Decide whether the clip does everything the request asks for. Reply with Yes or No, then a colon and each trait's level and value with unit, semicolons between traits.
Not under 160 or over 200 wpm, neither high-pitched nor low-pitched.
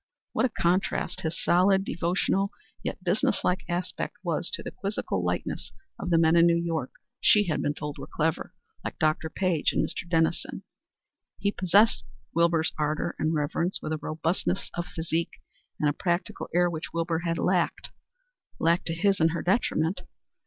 Yes: average, 170 wpm; medium, 170 Hz